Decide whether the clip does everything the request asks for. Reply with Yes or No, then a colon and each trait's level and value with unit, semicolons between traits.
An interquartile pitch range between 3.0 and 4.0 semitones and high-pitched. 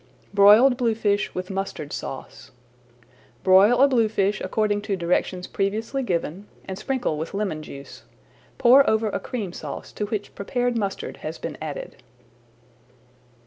Yes: average, 3.6 semitones; high, 205 Hz